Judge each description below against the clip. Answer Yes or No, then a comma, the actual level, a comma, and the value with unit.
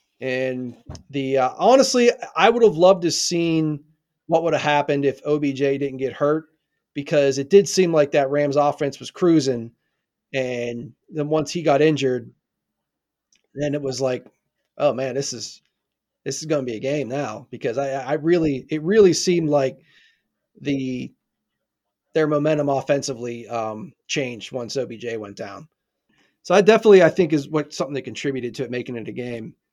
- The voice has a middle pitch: Yes, medium, 145 Hz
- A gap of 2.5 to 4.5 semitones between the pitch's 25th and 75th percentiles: Yes, average, 3.3 semitones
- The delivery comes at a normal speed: Yes, average, 170 wpm